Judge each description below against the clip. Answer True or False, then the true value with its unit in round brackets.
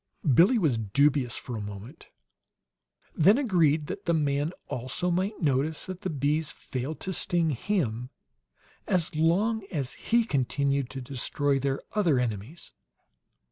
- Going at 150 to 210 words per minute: False (140 wpm)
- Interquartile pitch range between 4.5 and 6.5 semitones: True (5.1 semitones)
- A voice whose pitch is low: False (150 Hz)